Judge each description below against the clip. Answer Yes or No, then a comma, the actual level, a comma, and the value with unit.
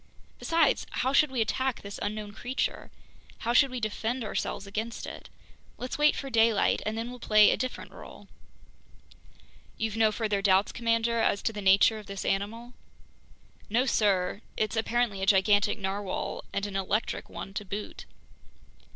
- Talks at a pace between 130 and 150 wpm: No, average, 160 wpm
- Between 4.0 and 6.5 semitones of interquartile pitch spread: No, average, 2.8 semitones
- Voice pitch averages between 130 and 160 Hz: No, high, 215 Hz